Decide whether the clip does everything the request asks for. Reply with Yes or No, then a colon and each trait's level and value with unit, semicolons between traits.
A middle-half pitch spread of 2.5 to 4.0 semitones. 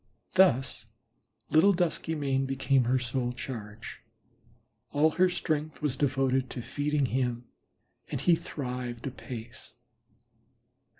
Yes: average, 3.3 semitones